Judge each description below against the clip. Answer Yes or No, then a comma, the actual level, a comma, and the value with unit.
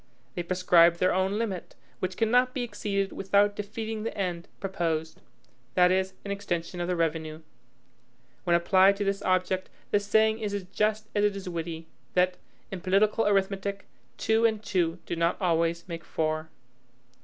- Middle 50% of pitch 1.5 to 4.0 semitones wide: Yes, average, 3.1 semitones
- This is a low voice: No, high, 190 Hz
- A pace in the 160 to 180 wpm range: Yes, average, 165 wpm